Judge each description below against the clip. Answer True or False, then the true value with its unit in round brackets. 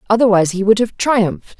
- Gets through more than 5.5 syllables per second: True (6.5 syllables/s)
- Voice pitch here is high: True (210 Hz)